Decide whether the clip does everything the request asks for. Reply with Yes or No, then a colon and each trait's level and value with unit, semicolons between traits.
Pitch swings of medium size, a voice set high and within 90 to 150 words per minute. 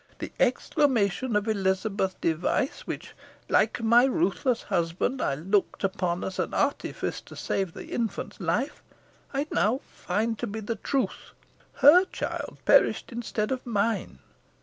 Yes: average, 4.4 semitones; high, 215 Hz; average, 140 wpm